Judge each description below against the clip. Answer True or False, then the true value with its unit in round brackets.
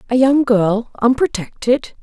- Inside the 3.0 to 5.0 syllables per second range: True (4.1 syllables/s)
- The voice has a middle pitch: False (240 Hz)